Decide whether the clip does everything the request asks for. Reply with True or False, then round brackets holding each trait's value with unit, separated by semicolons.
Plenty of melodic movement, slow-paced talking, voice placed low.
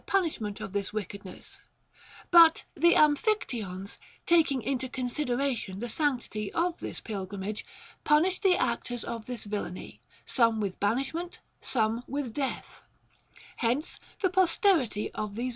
False (6.2 semitones; 115 wpm; 245 Hz)